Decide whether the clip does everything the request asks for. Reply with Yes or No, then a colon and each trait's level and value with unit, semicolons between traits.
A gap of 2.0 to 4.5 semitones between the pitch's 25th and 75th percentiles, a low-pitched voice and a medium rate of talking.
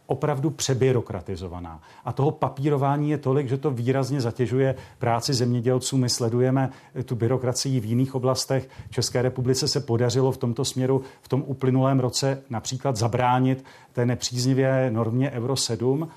No: narrow, 1.6 semitones; low, 130 Hz; average, 140 wpm